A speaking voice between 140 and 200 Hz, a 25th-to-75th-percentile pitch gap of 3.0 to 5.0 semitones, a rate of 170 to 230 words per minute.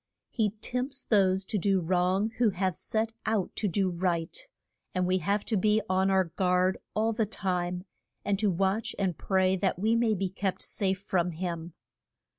No: high, 190 Hz; narrow, 2.5 semitones; average, 180 wpm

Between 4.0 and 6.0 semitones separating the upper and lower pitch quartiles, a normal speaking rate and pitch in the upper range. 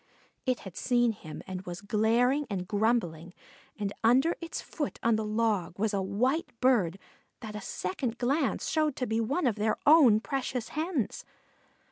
Yes: average, 4.3 semitones; average, 165 wpm; high, 225 Hz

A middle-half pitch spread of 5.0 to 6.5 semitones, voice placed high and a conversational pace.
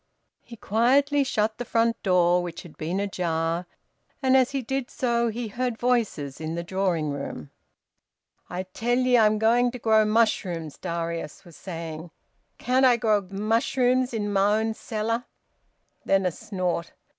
Yes: wide, 5.4 semitones; high, 215 Hz; average, 155 wpm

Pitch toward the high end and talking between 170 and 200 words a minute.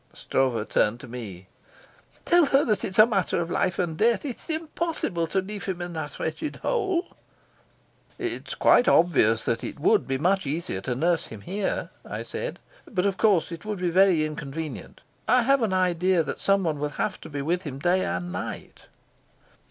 No: medium, 175 Hz; average, 185 wpm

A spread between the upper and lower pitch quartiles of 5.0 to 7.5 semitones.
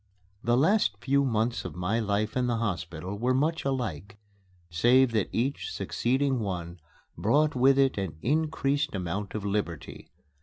Yes: wide, 5.6 semitones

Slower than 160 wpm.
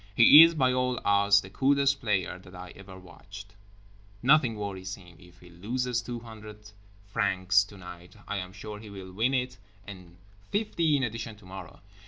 No: average, 170 wpm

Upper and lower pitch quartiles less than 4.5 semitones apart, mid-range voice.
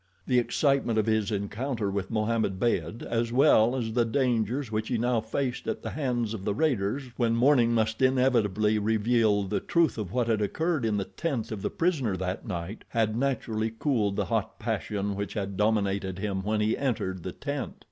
No: average, 3.3 semitones; low, 110 Hz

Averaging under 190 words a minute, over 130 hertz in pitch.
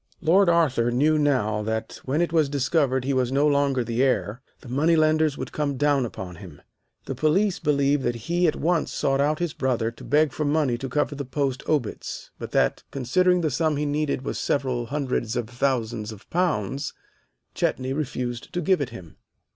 No: average, 195 wpm; medium, 140 Hz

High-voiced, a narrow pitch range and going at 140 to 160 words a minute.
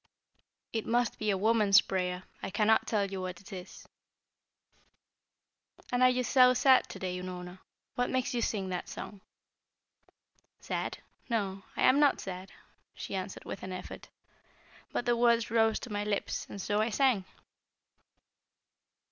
No: high, 210 Hz; average, 4.0 semitones; average, 155 wpm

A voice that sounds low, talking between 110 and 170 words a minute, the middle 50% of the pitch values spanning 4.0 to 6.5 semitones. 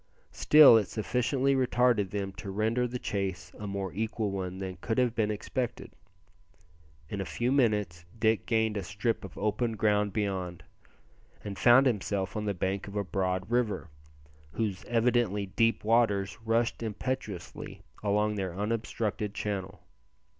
No: low, 105 Hz; average, 145 wpm; average, 3.0 semitones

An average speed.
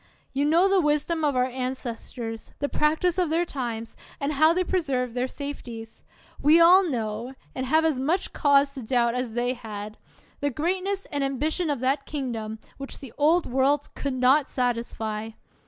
Yes: average, 170 wpm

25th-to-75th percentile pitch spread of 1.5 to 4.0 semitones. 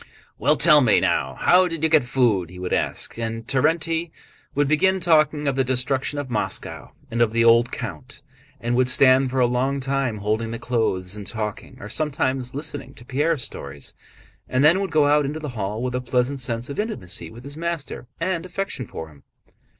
No: average, 4.4 semitones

